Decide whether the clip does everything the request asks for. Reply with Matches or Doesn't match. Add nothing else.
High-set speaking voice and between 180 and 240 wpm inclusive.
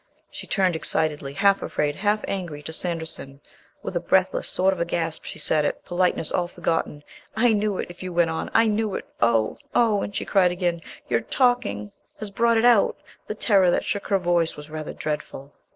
Doesn't match